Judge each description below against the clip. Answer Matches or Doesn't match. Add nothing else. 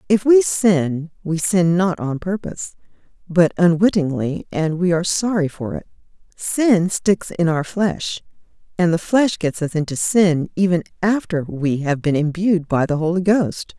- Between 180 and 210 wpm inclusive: Doesn't match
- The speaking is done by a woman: Matches